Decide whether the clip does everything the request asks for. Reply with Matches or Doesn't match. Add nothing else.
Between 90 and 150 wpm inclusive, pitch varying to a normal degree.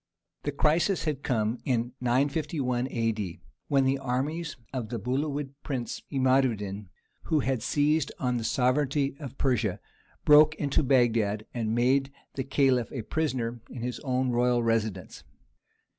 Matches